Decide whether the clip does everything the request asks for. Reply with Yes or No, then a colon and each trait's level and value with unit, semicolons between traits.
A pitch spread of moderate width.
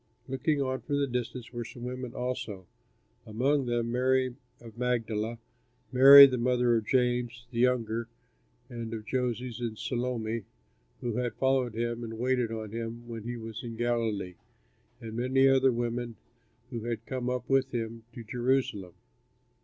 No: narrow, 1.8 semitones